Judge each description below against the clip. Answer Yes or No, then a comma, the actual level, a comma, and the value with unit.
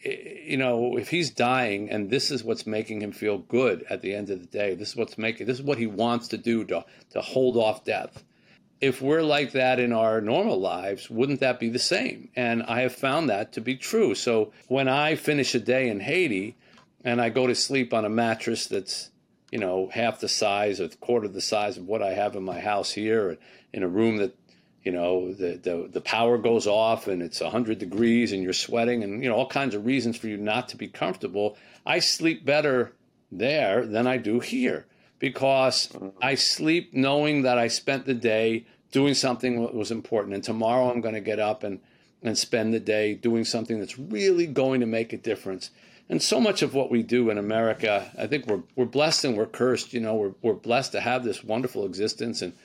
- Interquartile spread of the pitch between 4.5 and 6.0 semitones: No, average, 3.1 semitones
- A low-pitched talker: Yes, low, 120 Hz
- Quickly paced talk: Yes, fast, 220 wpm